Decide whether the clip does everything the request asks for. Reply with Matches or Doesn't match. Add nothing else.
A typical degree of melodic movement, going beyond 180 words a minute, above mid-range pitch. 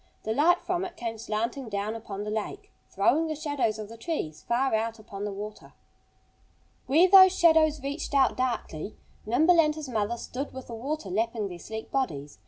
Doesn't match